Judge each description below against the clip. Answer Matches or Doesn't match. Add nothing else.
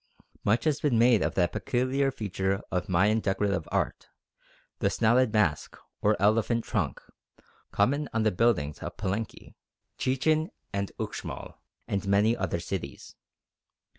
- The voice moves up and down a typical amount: Matches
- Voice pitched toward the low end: Matches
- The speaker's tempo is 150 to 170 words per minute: Doesn't match